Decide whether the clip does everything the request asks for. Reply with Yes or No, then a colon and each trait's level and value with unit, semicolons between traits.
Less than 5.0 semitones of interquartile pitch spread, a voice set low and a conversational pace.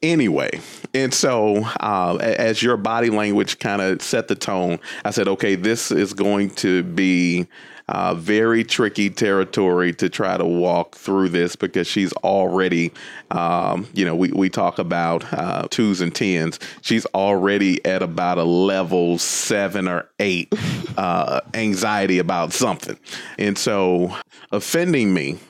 Yes: average, 2.7 semitones; very low, 95 Hz; average, 145 wpm